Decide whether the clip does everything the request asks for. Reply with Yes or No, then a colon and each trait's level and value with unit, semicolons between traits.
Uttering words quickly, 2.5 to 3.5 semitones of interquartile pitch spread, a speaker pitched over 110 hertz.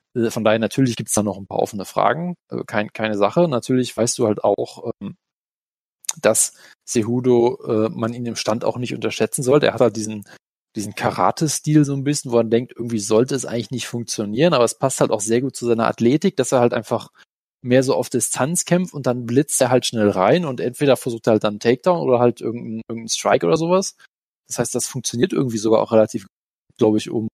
Yes: fast, 215 wpm; average, 2.8 semitones; low, 120 Hz